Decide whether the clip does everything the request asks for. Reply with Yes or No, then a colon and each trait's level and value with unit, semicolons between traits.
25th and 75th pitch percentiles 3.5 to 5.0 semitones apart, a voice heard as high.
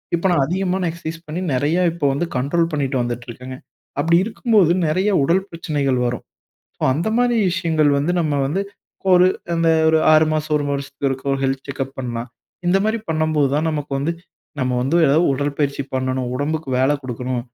No: average, 3.9 semitones; medium, 150 Hz